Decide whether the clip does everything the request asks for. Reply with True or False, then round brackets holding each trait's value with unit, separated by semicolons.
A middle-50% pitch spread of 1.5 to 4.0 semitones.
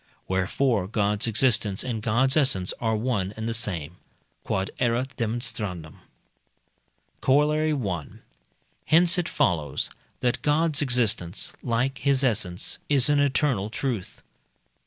False (5.6 semitones)